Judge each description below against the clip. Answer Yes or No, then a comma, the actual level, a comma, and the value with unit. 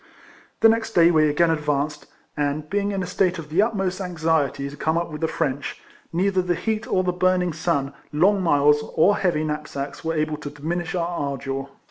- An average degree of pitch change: Yes, average, 3.5 semitones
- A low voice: No, medium, 165 Hz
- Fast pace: No, average, 195 wpm